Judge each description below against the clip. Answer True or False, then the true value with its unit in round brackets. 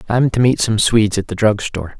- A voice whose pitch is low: True (110 Hz)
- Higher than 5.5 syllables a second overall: True (6.1 syllables/s)